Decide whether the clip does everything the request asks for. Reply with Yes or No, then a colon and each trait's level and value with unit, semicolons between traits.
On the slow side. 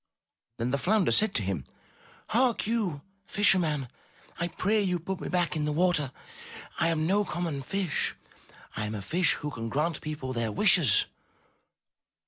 No: average, 165 wpm